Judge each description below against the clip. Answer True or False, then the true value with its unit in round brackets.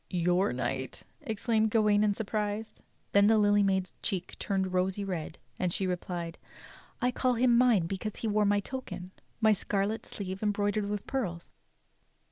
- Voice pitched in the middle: False (205 Hz)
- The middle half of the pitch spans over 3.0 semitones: False (2.7 semitones)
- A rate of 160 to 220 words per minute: True (165 wpm)